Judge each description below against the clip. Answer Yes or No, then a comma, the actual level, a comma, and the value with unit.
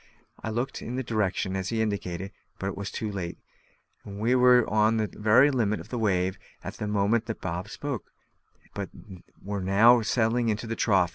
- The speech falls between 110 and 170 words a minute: No, average, 180 wpm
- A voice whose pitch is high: No, low, 110 Hz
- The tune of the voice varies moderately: Yes, average, 3.0 semitones